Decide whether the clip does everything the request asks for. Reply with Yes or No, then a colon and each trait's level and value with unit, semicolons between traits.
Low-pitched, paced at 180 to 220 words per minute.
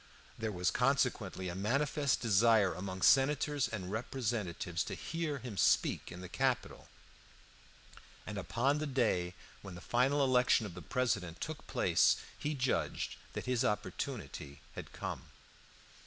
No: low, 115 Hz; average, 140 wpm